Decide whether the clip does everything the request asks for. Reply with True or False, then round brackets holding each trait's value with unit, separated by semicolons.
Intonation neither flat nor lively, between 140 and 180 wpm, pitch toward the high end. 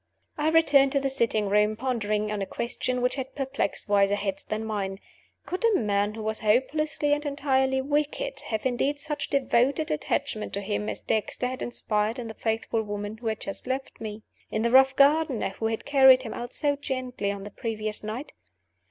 False (4.4 semitones; 195 wpm; 240 Hz)